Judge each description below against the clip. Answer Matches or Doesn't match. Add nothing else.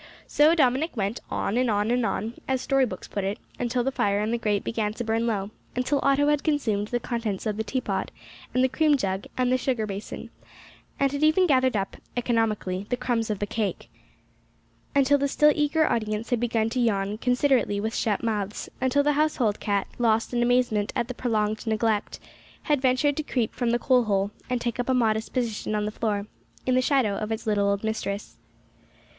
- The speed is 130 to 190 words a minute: Doesn't match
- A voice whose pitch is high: Matches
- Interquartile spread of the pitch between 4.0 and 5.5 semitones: Doesn't match